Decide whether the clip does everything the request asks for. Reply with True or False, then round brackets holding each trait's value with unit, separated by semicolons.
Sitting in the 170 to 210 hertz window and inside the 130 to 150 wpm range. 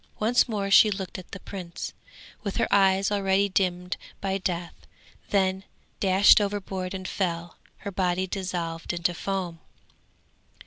True (190 Hz; 135 wpm)